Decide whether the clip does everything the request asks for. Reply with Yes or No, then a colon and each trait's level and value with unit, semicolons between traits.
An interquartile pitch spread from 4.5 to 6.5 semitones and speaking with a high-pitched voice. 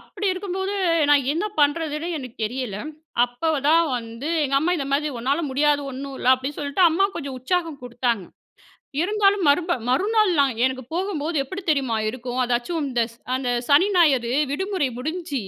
Yes: average, 5.0 semitones; very high, 285 Hz